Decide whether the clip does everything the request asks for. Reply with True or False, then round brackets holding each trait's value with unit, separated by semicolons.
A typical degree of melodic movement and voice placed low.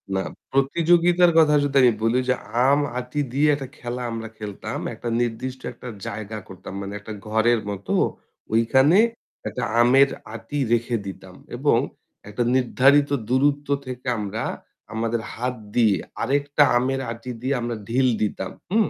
True (3.7 semitones; 125 Hz)